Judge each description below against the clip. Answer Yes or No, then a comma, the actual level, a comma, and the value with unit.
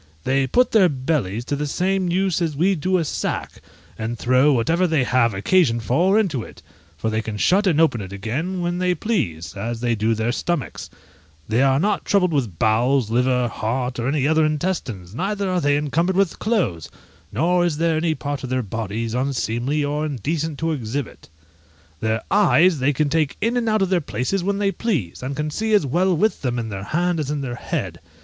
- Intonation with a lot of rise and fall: Yes, wide, 6.9 semitones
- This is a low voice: No, medium, 145 Hz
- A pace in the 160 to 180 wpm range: No, fast, 205 wpm